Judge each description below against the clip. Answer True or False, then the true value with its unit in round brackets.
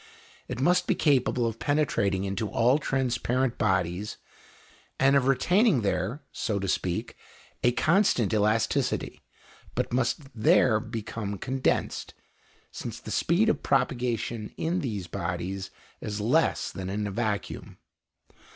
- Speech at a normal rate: False (125 wpm)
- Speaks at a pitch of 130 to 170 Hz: False (120 Hz)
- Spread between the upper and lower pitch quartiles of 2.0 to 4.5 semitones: False (4.9 semitones)